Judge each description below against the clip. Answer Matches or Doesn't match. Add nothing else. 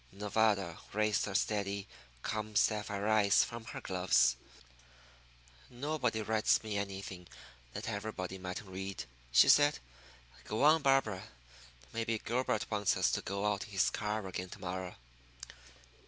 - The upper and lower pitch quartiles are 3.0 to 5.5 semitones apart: Doesn't match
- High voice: Doesn't match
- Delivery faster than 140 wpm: Doesn't match